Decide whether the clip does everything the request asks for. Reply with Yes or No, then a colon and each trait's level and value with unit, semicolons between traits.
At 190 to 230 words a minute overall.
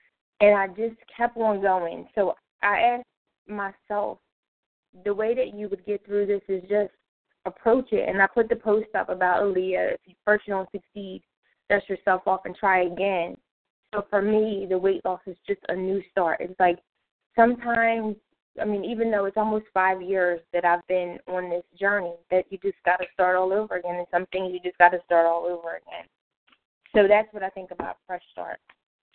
Yes: average, 200 wpm